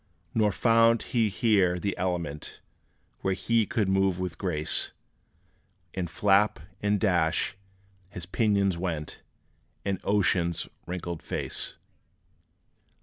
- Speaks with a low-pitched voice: Yes, very low, 95 Hz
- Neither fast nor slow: No, slow, 105 wpm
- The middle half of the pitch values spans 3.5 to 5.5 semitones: No, average, 2.9 semitones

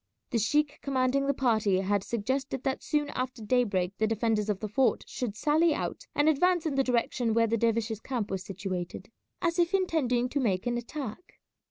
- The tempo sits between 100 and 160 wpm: No, average, 190 wpm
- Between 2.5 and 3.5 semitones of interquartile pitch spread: No, average, 4.6 semitones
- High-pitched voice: Yes, high, 240 Hz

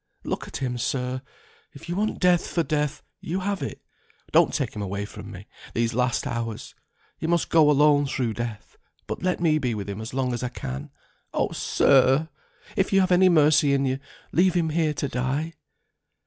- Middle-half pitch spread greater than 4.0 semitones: Yes, average, 5.1 semitones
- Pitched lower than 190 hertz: Yes, medium, 140 Hz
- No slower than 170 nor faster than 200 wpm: Yes, average, 195 wpm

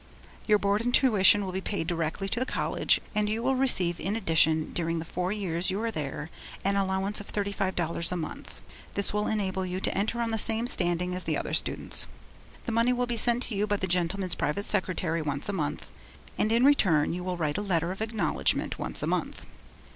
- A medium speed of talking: No, fast, 220 wpm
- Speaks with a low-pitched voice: No, high, 195 Hz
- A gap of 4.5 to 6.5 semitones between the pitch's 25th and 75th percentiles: No, average, 3.7 semitones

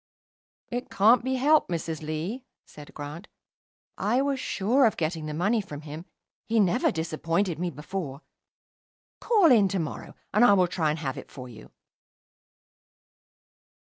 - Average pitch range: No, wide, 6.6 semitones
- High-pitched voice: No, medium, 180 Hz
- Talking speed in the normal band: Yes, average, 150 wpm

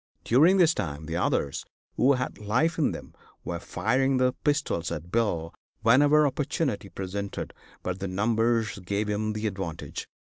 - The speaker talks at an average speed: Yes, average, 150 wpm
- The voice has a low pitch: Yes, low, 110 Hz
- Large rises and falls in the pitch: Yes, wide, 6.2 semitones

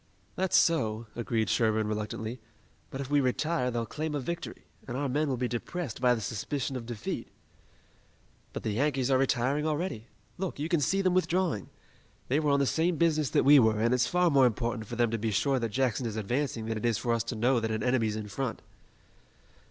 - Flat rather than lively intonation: No, average, 4.6 semitones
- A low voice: Yes, low, 125 Hz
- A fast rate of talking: Yes, fast, 215 wpm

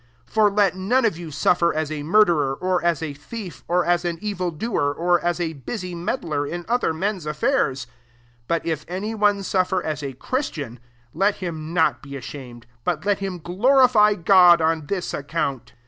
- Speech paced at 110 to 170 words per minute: No, average, 190 wpm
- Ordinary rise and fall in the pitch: Yes, average, 4.6 semitones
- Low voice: No, medium, 175 Hz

